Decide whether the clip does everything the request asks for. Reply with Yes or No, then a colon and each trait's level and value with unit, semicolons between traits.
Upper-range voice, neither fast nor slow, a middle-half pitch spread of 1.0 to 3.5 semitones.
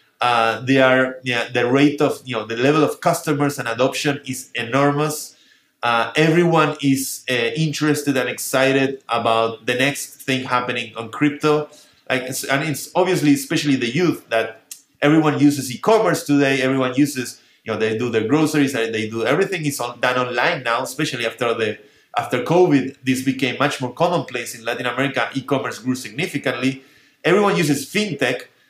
No: low, 135 Hz; average, 165 wpm; average, 3.1 semitones